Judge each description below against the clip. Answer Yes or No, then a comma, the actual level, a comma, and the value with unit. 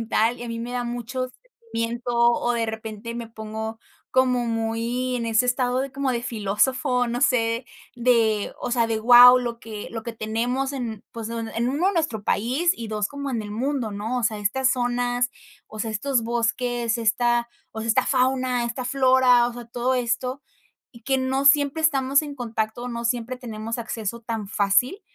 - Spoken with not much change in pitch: Yes, narrow, 2.0 semitones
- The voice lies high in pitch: Yes, high, 240 Hz